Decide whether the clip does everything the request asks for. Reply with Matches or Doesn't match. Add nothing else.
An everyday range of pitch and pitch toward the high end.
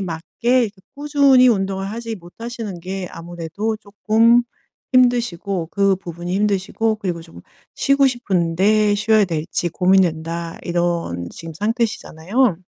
Matches